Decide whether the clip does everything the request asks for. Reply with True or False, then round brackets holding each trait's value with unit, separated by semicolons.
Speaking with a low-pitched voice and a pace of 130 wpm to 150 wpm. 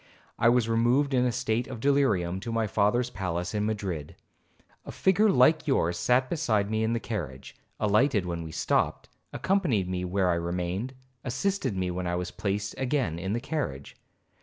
False (110 Hz; 180 wpm)